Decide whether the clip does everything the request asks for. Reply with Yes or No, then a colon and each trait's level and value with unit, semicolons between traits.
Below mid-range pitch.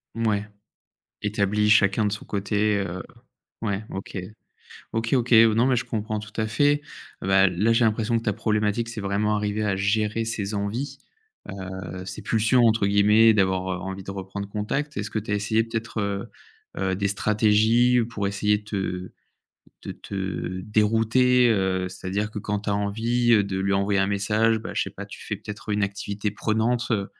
Yes: low, 105 Hz